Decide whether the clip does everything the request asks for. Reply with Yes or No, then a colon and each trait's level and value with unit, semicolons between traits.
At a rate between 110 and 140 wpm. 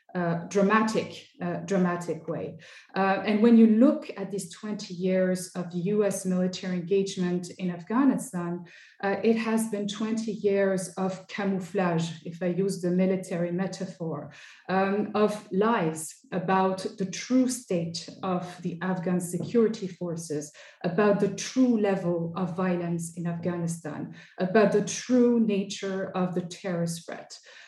Yes: slow, 135 wpm